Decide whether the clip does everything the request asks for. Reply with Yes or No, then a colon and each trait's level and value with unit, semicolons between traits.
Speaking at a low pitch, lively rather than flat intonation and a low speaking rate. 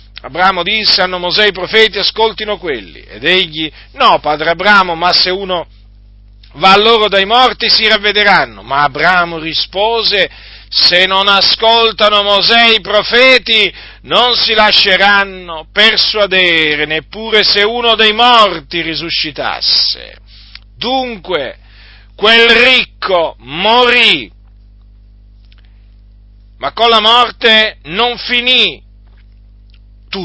No: high, 190 Hz; wide, 7.8 semitones; slow, 105 wpm